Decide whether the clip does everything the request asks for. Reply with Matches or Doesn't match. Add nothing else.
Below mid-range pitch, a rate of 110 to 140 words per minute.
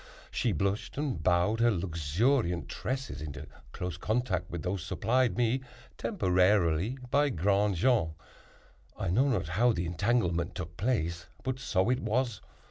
Matches